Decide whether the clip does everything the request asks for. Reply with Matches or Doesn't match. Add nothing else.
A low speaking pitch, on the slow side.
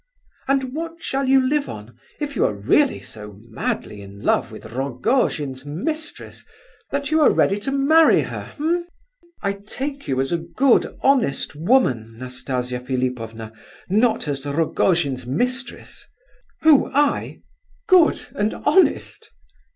Doesn't match